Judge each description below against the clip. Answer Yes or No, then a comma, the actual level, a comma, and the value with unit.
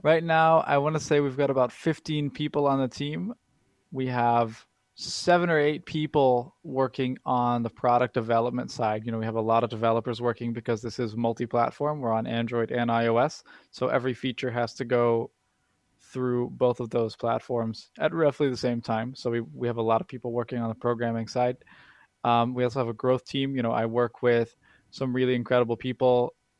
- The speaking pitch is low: Yes, low, 125 Hz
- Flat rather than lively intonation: Yes, narrow, 2.2 semitones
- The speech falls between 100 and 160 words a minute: No, average, 200 wpm